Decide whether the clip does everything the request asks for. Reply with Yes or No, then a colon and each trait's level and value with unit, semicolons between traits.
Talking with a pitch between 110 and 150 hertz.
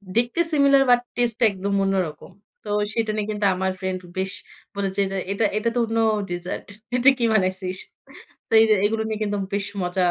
No: high, 205 Hz